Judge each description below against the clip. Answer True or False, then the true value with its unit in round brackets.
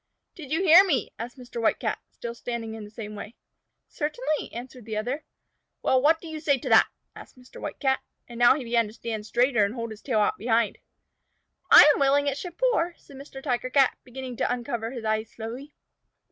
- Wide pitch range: False (3.8 semitones)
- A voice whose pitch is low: False (250 Hz)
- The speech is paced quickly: True (215 wpm)